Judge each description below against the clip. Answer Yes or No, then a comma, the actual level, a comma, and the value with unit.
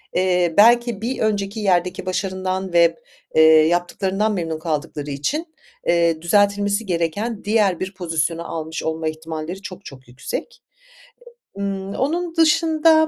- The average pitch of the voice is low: No, medium, 185 Hz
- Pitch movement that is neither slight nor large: Yes, average, 4.4 semitones